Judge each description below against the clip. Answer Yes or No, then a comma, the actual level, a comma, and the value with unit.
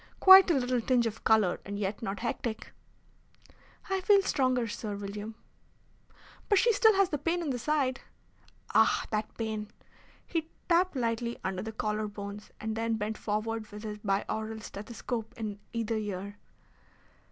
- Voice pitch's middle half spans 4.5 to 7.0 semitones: No, average, 3.5 semitones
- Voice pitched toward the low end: No, high, 225 Hz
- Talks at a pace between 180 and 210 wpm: No, average, 155 wpm